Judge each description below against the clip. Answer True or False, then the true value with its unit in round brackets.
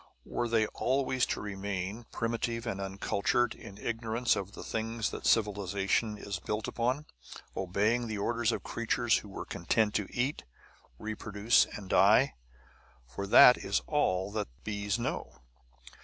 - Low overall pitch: True (110 Hz)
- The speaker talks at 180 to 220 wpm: False (140 wpm)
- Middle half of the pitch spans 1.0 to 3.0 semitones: True (2.7 semitones)